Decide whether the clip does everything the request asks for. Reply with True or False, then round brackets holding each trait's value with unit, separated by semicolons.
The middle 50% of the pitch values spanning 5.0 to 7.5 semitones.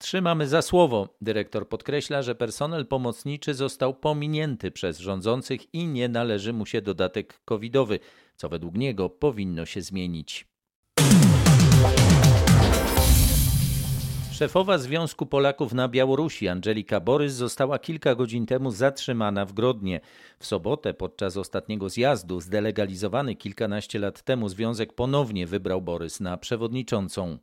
True (5.5 semitones)